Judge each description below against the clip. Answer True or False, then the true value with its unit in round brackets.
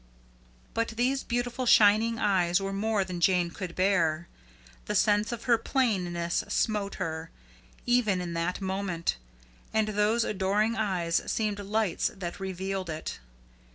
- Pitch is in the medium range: False (200 Hz)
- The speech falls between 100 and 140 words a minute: True (135 wpm)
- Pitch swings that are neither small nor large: True (3.6 semitones)